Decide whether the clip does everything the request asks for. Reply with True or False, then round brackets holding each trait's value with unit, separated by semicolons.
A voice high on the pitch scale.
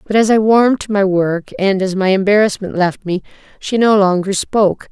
True (200 Hz)